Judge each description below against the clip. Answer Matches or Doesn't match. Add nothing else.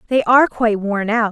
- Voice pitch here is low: Doesn't match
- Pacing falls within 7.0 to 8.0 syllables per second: Doesn't match